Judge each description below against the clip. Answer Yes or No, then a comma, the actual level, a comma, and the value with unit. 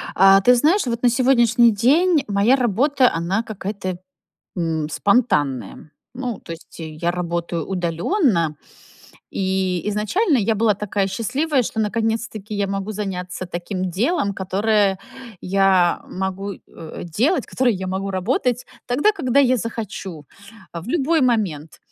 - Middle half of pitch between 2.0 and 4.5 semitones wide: No, average, 4.9 semitones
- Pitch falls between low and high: No, high, 205 Hz